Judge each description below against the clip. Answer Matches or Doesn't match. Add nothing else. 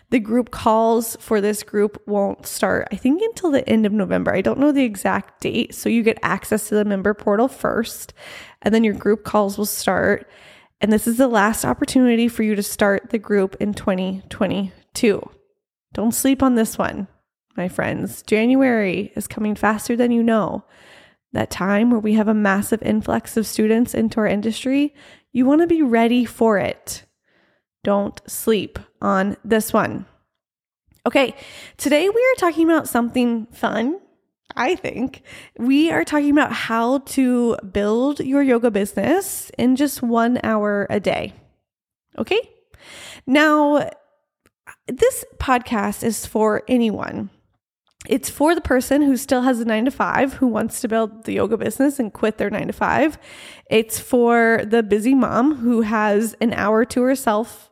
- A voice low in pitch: Doesn't match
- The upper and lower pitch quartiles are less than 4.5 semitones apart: Matches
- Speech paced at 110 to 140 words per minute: Doesn't match